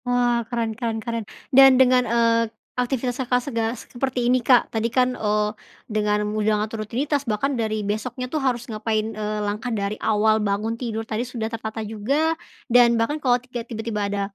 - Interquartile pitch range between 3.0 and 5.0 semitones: No, narrow, 2.5 semitones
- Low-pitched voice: No, high, 230 Hz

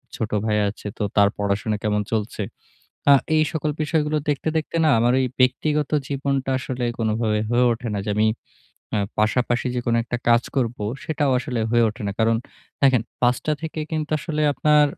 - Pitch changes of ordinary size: Yes, average, 5.0 semitones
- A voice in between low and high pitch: No, low, 125 Hz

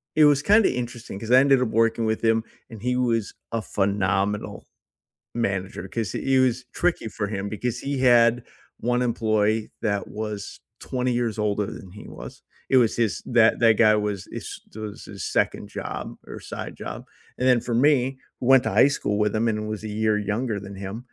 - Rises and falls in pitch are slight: No, average, 3.0 semitones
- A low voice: Yes, low, 115 Hz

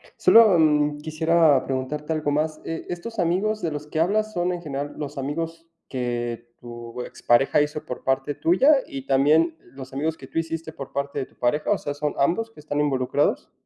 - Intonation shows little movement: No, average, 3.3 semitones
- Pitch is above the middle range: No, medium, 150 Hz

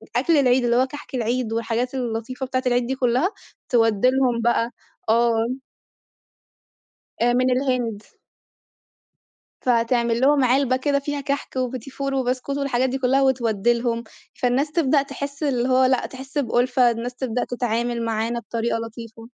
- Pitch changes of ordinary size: No, narrow, 2.1 semitones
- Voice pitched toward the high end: Yes, very high, 250 Hz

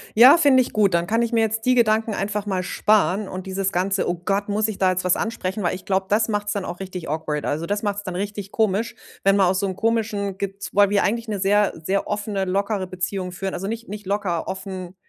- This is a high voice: Yes, high, 200 Hz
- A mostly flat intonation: Yes, narrow, 2.2 semitones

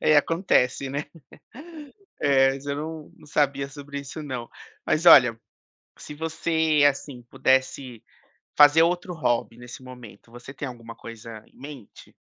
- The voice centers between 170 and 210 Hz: No, medium, 140 Hz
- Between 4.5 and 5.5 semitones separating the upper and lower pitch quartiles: No, average, 3.4 semitones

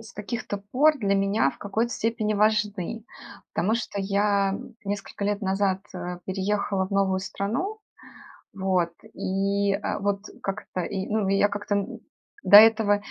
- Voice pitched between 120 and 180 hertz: No, high, 200 Hz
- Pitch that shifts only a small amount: Yes, narrow, 1.4 semitones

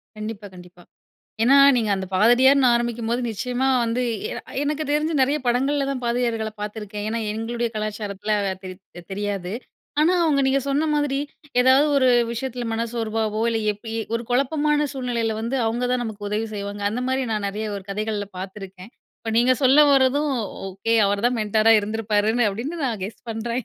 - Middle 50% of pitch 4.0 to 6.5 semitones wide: No, average, 3.6 semitones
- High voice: Yes, high, 230 Hz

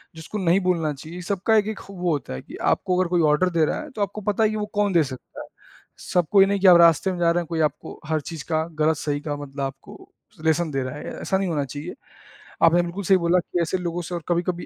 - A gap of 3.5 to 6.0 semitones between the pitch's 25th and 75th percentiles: No, average, 3.0 semitones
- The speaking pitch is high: No, medium, 175 Hz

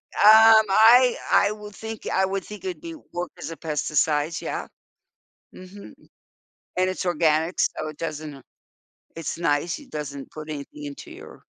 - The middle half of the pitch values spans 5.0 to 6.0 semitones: Yes, wide, 5.6 semitones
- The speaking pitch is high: No, medium, 175 Hz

